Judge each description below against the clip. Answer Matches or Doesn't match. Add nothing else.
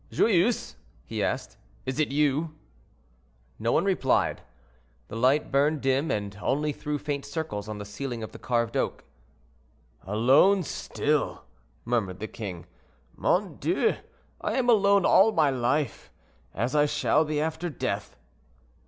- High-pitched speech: Doesn't match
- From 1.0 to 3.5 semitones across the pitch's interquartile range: Doesn't match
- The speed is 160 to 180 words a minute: Doesn't match